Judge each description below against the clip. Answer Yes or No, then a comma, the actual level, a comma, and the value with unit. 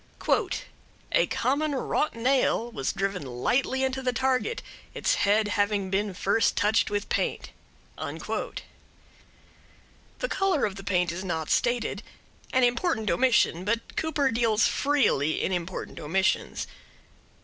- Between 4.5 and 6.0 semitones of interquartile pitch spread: Yes, wide, 5.4 semitones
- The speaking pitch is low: No, high, 220 Hz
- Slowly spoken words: Yes, slow, 125 wpm